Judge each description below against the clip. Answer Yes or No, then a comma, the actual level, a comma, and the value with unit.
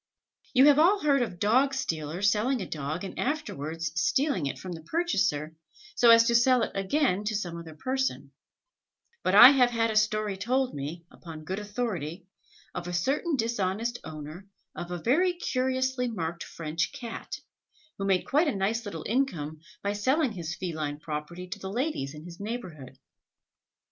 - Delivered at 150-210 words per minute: Yes, average, 170 wpm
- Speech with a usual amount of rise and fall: No, wide, 7.3 semitones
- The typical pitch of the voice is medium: No, high, 205 Hz